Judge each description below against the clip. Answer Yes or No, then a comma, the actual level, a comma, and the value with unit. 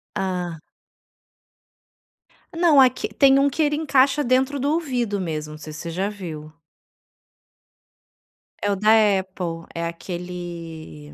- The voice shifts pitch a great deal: Yes, wide, 8.2 semitones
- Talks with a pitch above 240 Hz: No, high, 190 Hz